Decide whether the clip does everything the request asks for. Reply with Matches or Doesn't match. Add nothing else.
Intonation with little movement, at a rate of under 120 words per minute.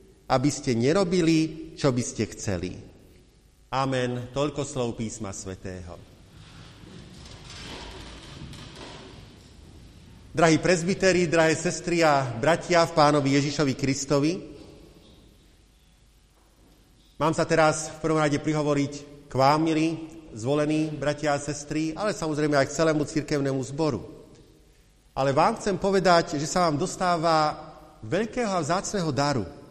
Doesn't match